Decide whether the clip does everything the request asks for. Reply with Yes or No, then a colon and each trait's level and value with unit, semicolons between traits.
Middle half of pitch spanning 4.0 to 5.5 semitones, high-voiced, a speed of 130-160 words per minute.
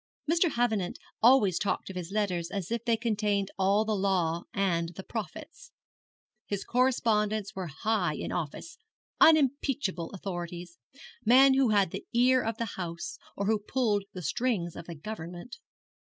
Yes: average, 4.7 semitones; high, 205 Hz; average, 155 wpm